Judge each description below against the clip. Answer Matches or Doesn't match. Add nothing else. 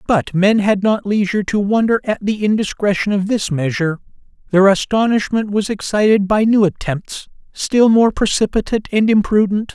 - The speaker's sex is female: Doesn't match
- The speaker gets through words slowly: Doesn't match